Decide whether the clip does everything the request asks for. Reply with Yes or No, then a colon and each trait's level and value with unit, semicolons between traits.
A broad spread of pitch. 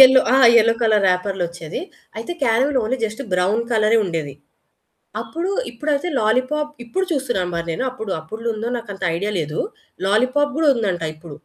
Yes: wide, 6.0 semitones